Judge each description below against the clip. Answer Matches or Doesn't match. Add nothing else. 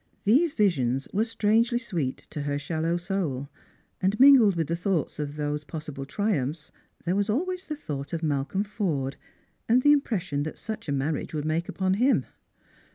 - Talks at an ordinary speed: Matches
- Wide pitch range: Matches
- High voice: Doesn't match